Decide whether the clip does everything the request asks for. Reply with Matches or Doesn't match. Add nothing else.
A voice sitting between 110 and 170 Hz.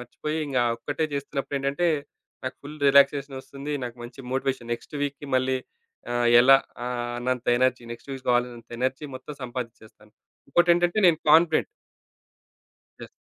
Matches